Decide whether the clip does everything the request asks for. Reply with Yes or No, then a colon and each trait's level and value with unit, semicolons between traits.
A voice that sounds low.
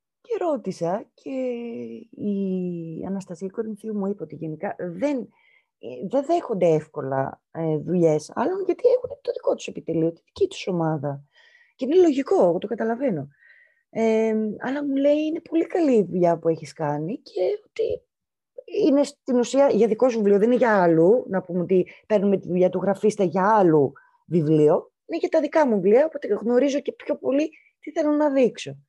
No: high, 230 Hz